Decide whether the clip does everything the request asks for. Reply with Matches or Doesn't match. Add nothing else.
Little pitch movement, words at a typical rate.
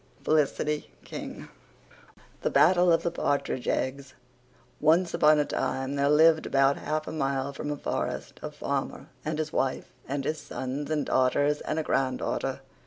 Matches